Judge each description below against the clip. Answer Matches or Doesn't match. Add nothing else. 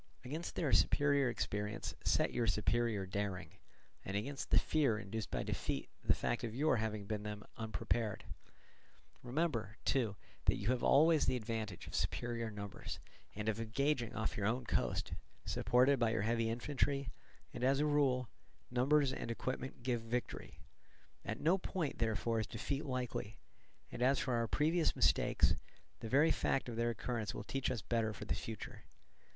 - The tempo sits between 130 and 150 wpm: Doesn't match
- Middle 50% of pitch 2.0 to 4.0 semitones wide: Matches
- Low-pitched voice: Matches